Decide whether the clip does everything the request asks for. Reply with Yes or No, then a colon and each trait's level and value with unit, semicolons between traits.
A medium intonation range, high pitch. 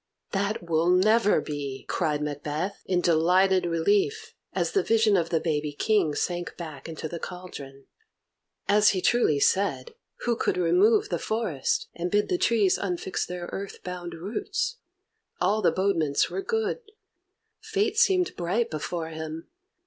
No: average, 4.8 semitones; medium, 180 Hz